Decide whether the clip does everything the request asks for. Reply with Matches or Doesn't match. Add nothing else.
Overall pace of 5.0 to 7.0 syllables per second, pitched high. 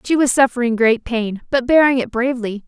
Matches